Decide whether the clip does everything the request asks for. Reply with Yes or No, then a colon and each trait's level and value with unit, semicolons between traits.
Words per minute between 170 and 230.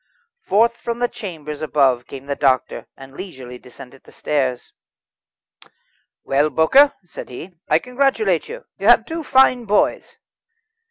No: average, 140 wpm